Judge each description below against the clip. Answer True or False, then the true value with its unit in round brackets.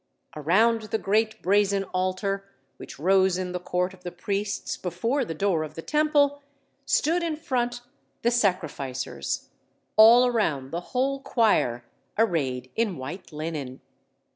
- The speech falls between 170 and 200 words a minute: False (140 wpm)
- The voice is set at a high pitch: True (195 Hz)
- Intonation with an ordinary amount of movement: False (5.8 semitones)